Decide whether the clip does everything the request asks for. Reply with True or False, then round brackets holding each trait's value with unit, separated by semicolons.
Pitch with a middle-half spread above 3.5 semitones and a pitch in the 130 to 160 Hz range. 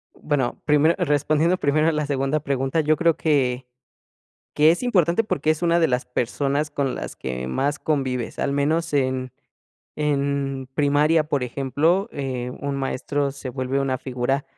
False (2.6 semitones; 140 Hz)